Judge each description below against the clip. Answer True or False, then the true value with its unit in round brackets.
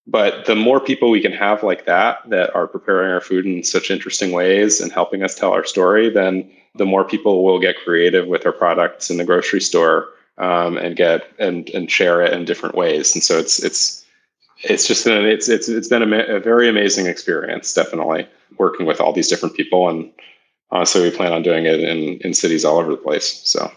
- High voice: False (105 Hz)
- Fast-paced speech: True (220 wpm)